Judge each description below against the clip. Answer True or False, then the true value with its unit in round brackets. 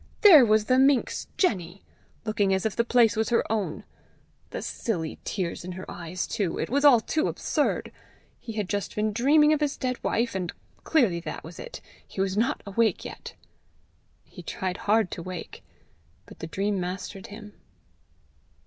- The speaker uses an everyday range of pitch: True (4.5 semitones)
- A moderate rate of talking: True (175 wpm)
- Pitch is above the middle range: True (210 Hz)